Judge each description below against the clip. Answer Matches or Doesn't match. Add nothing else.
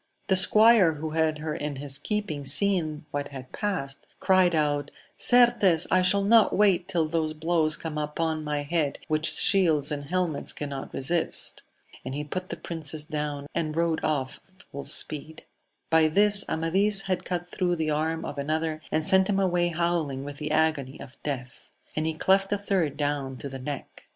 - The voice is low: Doesn't match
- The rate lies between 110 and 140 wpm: Doesn't match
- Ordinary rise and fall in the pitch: Matches